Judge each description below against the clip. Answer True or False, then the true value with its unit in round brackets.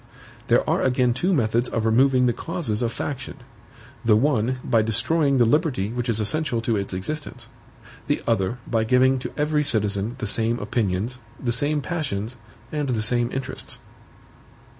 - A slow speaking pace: False (160 wpm)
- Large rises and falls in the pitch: False (3.8 semitones)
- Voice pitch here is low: True (120 Hz)